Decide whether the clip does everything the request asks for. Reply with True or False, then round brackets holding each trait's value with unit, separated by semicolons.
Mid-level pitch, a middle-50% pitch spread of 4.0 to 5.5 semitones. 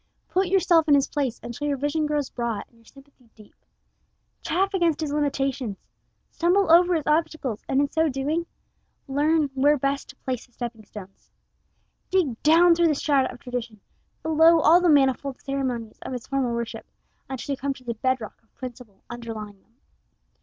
False (275 Hz; 4.6 semitones)